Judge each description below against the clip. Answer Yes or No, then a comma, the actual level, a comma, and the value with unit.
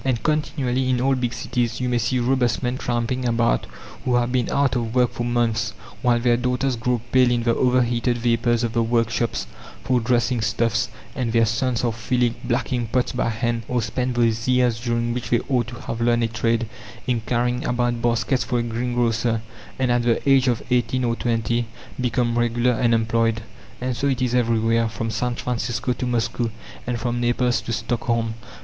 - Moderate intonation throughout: No, narrow, 1.3 semitones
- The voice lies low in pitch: Yes, low, 120 Hz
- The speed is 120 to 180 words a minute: No, average, 190 wpm